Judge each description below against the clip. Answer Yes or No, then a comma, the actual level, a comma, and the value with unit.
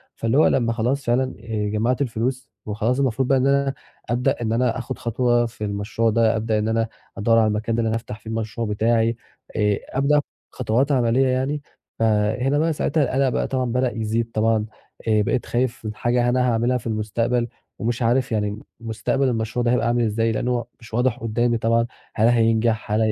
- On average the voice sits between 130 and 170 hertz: No, low, 115 Hz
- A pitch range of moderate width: No, narrow, 2.1 semitones